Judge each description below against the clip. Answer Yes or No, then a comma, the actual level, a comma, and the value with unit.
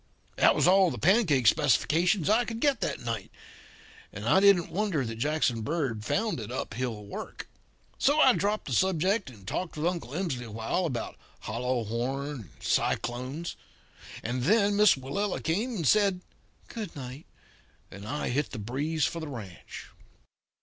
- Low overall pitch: No, medium, 150 Hz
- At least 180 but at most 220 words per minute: No, average, 165 wpm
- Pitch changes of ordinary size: No, wide, 7.9 semitones